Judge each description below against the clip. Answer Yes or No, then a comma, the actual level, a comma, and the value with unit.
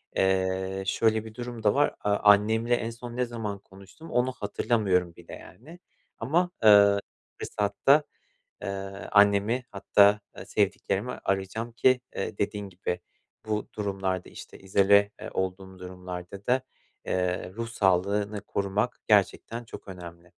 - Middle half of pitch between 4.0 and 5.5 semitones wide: No, average, 3.2 semitones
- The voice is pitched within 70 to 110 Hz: Yes, low, 100 Hz